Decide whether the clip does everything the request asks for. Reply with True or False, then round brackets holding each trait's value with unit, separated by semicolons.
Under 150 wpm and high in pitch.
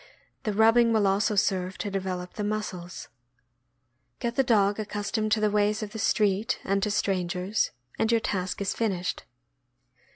False (175 wpm; 205 Hz)